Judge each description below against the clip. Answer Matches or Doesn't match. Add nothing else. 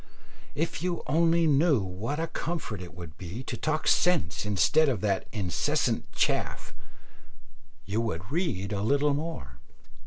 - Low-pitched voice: Matches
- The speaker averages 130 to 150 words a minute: Matches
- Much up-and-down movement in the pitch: Matches